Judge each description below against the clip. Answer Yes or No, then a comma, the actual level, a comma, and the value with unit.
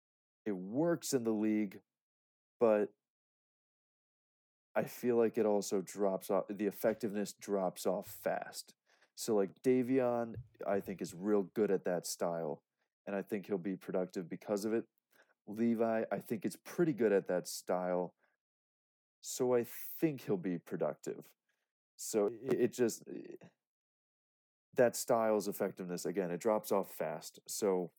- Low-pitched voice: Yes, low, 105 Hz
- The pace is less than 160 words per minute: Yes, average, 140 wpm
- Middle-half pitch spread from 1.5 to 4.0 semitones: Yes, average, 3.5 semitones